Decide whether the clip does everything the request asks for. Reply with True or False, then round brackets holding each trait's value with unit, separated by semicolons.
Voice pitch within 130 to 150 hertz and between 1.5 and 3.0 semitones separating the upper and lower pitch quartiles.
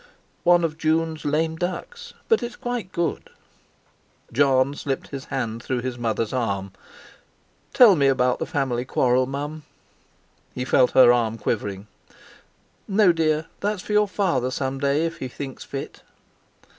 False (140 Hz; 4.8 semitones)